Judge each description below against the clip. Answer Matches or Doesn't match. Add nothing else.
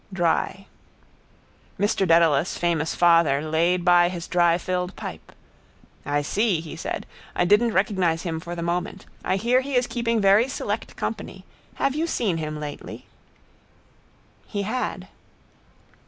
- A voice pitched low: Doesn't match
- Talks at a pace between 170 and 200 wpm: Doesn't match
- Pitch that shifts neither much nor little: Matches